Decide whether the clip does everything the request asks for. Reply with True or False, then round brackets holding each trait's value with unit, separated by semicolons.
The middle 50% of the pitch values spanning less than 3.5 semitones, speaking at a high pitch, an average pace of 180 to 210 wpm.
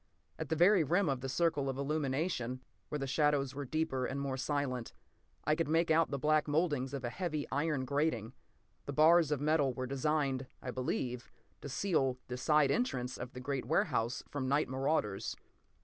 False (3.0 semitones; 140 Hz; 185 wpm)